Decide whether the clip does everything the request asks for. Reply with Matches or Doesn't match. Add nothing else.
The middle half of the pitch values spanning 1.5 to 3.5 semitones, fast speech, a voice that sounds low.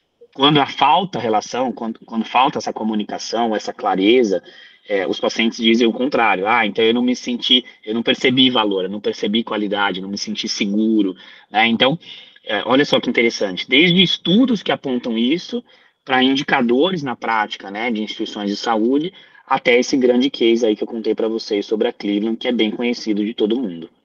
Matches